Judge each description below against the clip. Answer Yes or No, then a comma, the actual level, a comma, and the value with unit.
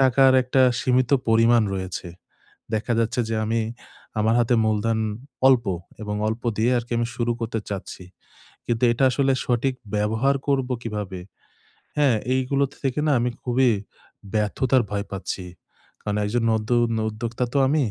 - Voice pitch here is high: No, low, 120 Hz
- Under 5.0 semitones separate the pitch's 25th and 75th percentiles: Yes, average, 2.9 semitones